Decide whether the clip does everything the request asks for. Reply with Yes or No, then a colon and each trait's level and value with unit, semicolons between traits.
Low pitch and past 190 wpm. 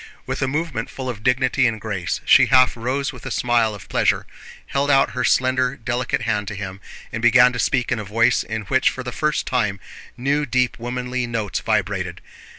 Yes: low, 120 Hz; average, 200 wpm